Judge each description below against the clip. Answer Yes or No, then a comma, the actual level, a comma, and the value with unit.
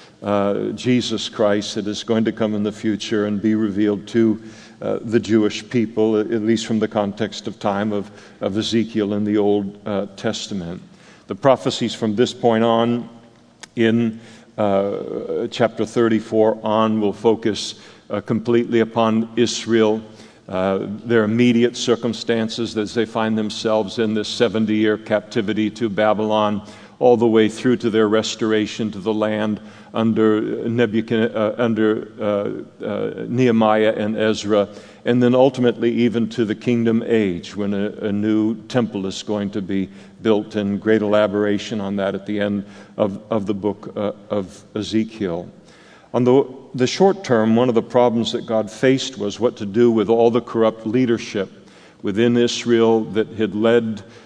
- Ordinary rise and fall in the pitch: No, narrow, 1.7 semitones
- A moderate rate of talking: Yes, average, 160 wpm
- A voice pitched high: No, low, 110 Hz